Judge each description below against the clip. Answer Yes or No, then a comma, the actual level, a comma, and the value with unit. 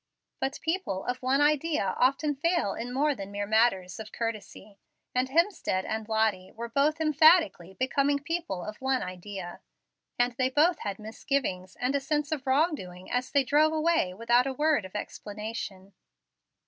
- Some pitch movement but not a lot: No, wide, 6.4 semitones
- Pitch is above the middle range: Yes, very high, 255 Hz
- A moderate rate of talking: Yes, average, 160 wpm